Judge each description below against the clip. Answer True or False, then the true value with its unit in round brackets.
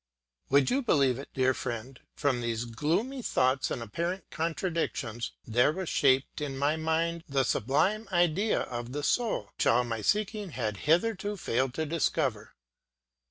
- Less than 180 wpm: True (155 wpm)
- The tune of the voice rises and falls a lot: True (5.9 semitones)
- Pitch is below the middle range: False (145 Hz)